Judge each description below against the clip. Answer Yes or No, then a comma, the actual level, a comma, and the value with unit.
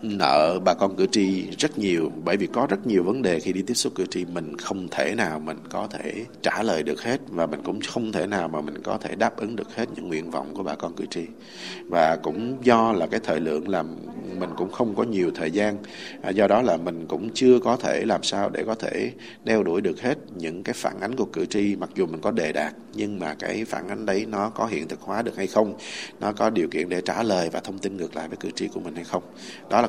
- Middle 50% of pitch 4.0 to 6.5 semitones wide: Yes, average, 5.2 semitones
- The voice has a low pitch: Yes, very low, 95 Hz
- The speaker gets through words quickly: Yes, fast, 265 wpm